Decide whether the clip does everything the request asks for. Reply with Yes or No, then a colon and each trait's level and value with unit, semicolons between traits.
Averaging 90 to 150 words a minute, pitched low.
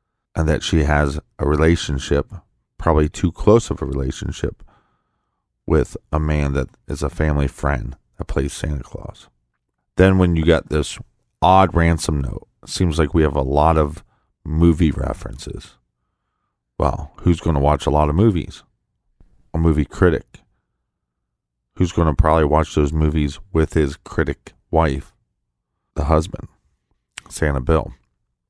Yes: average, 140 wpm; very low, 75 Hz